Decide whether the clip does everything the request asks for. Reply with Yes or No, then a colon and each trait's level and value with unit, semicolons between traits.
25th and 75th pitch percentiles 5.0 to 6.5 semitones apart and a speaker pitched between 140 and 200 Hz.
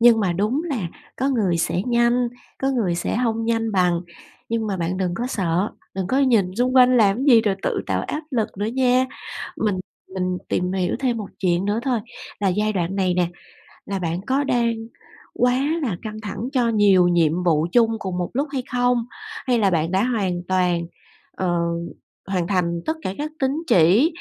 No: average, 5.3 semitones; high, 210 Hz